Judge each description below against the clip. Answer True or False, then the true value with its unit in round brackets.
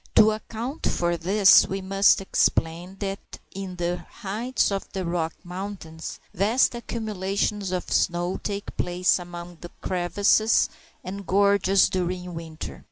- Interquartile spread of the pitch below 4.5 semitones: True (2.4 semitones)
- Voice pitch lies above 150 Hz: True (190 Hz)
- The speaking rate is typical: False (130 wpm)